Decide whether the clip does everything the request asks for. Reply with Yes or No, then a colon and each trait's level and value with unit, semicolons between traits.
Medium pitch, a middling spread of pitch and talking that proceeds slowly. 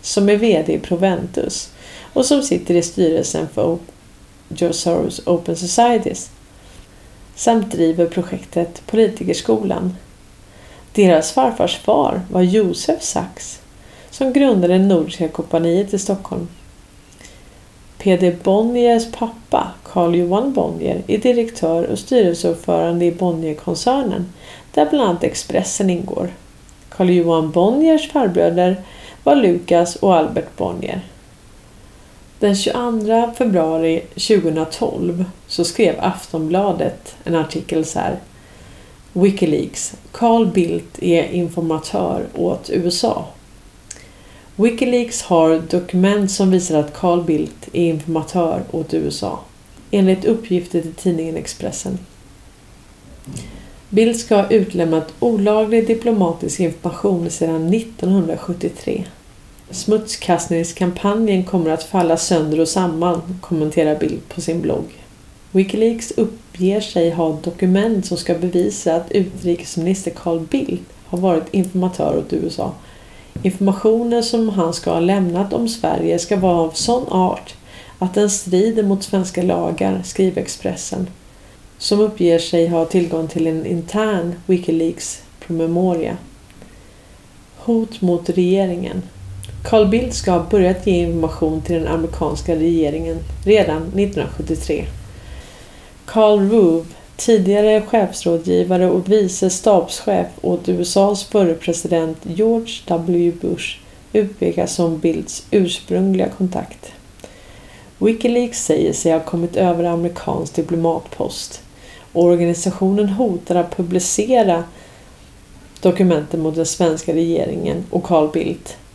Yes: medium, 175 Hz; average, 3.6 semitones; slow, 110 wpm